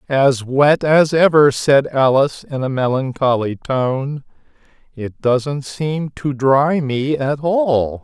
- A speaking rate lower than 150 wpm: Yes, slow, 135 wpm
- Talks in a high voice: No, medium, 140 Hz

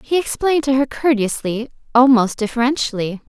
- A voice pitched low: No, very high, 250 Hz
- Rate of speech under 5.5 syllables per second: No, 5.6 syllables/s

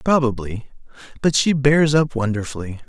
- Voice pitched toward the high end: No, low, 130 Hz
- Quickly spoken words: No, slow, 125 wpm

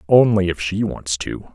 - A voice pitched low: Yes, very low, 90 Hz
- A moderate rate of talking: Yes, average, 195 wpm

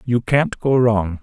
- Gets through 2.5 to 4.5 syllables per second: Yes, 3.5 syllables/s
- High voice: No, low, 115 Hz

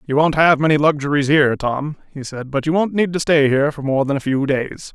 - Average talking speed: No, fast, 265 wpm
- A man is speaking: Yes, male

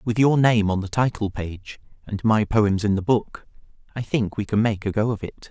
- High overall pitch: No, low, 105 Hz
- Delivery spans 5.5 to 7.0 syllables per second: No, 4.9 syllables/s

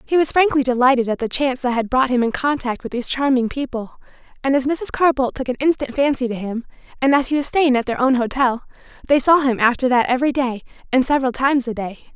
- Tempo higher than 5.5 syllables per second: Yes, 6.5 syllables/s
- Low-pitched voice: No, very high, 260 Hz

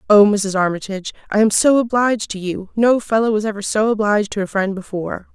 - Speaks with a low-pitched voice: No, high, 210 Hz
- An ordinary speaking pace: No, fast, 215 wpm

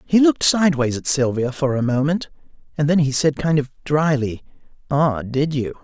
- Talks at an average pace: Yes, average, 185 wpm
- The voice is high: No, medium, 140 Hz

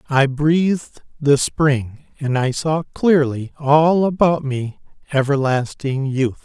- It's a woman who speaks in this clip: No, male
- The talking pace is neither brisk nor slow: No, slow, 120 wpm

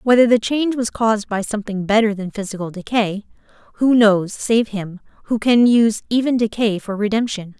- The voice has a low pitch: No, high, 215 Hz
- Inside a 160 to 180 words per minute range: Yes, average, 175 wpm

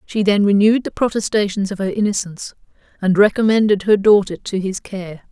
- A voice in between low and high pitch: No, high, 200 Hz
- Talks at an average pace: Yes, average, 170 wpm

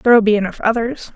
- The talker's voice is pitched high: Yes, high, 225 Hz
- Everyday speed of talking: No, fast, 210 wpm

